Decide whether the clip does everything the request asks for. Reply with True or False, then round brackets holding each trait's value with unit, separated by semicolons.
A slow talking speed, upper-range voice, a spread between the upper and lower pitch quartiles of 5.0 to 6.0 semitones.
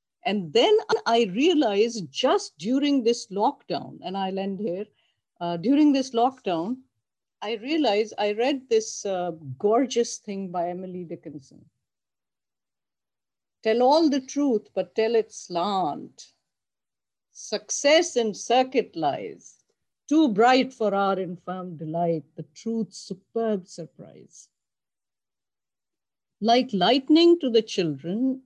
True (115 wpm; 220 Hz; 5.6 semitones)